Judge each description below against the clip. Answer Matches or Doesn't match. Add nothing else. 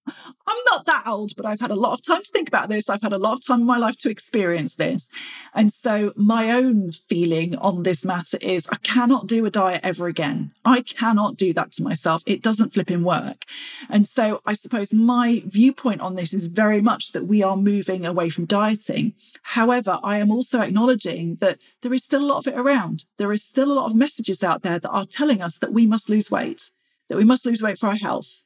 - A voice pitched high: Matches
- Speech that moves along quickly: Matches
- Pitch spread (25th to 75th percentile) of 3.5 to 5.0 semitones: Matches